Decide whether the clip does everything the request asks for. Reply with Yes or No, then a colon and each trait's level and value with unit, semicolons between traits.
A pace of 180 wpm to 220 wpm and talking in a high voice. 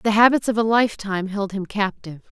Yes: average, 200 wpm; high, 205 Hz